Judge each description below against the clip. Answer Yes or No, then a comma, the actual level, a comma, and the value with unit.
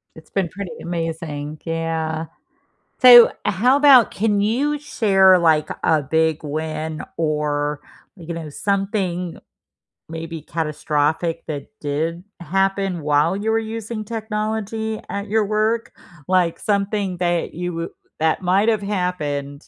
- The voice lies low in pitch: No, medium, 175 Hz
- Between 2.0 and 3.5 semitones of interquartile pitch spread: No, average, 4.7 semitones